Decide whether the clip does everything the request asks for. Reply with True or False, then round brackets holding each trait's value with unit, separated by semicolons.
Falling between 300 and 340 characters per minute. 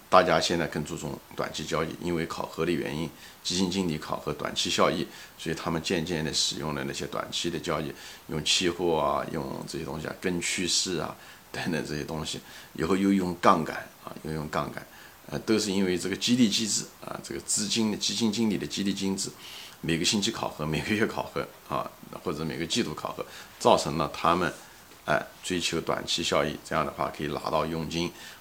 True (305 characters per minute)